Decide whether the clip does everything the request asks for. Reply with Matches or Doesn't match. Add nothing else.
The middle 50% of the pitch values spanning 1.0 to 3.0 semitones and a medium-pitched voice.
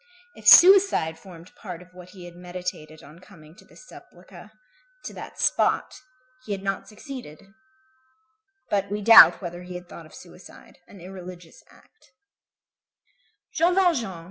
Matches